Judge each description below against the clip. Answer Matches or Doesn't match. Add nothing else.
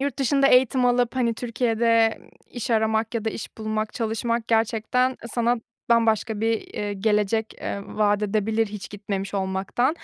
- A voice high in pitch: Matches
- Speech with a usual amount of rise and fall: Doesn't match